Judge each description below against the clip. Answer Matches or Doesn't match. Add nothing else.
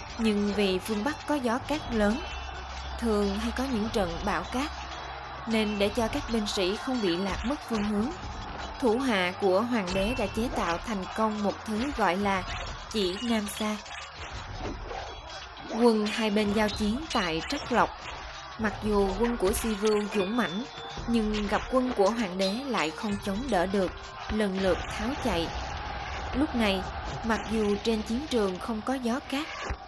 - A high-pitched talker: Matches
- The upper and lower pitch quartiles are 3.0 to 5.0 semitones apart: Doesn't match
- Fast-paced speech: Doesn't match